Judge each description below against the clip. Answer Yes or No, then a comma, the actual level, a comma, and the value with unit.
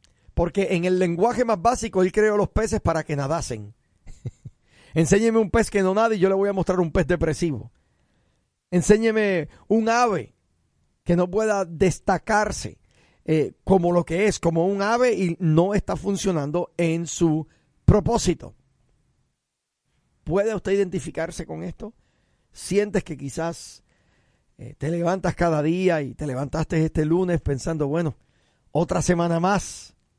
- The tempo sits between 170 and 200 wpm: No, average, 145 wpm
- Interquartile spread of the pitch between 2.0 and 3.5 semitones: No, average, 3.9 semitones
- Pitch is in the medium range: Yes, medium, 175 Hz